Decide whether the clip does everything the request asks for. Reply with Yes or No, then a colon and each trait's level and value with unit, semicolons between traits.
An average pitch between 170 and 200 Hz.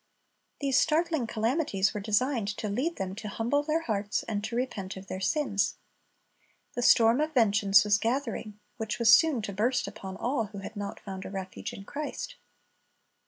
No: high, 225 Hz